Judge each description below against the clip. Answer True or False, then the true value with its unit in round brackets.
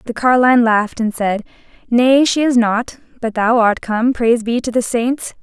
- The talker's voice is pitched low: False (235 Hz)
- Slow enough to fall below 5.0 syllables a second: True (4.8 syllables/s)